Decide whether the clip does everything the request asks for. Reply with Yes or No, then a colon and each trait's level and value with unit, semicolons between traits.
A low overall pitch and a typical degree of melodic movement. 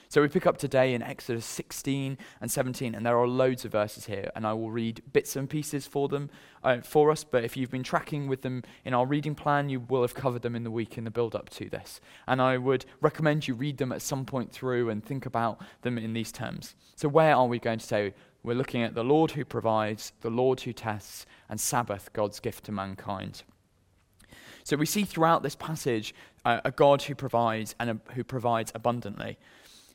Yes: low, 125 Hz; average, 3.6 semitones